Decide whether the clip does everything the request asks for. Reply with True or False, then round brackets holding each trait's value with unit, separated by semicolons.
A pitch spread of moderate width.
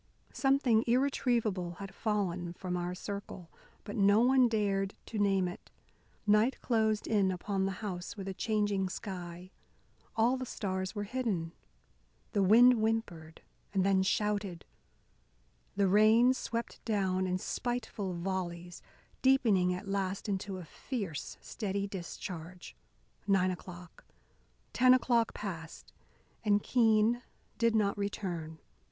True (3.3 semitones)